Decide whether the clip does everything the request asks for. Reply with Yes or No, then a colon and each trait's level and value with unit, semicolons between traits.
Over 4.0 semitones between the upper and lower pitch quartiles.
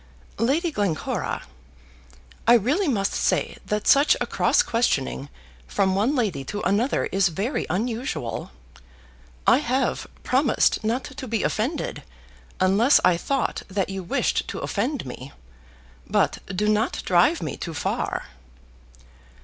Yes: wide, 5.5 semitones